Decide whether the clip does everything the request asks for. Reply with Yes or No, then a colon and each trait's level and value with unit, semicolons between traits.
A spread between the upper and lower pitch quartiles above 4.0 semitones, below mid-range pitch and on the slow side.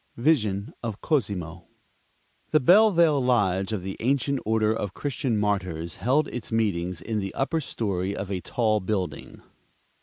No: wide, 5.4 semitones; low, 110 Hz; average, 145 wpm